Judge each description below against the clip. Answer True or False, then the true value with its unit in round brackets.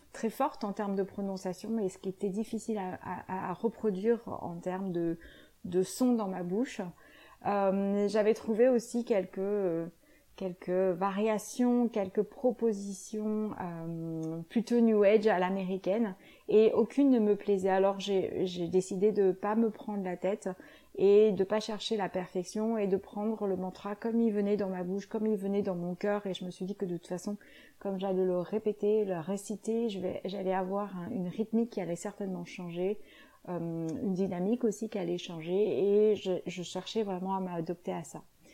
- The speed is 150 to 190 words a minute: True (185 wpm)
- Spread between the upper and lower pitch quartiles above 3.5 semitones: False (2.6 semitones)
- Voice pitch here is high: True (200 Hz)